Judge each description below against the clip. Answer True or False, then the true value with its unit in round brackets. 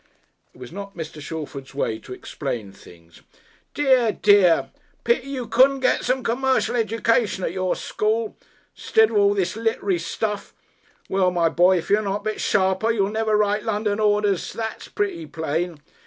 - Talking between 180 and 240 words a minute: False (165 wpm)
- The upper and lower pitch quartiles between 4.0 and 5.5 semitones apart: True (4.3 semitones)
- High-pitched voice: True (205 Hz)